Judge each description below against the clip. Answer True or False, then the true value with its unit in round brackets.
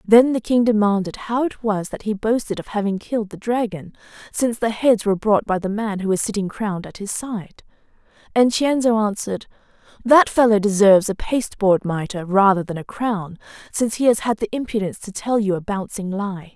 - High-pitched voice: True (210 Hz)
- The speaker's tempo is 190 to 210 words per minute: True (200 wpm)